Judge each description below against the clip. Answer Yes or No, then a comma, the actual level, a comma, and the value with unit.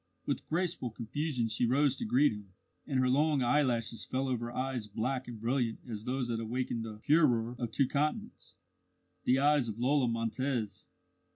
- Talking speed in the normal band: Yes, average, 170 wpm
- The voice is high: No, low, 125 Hz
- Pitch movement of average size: Yes, average, 3.3 semitones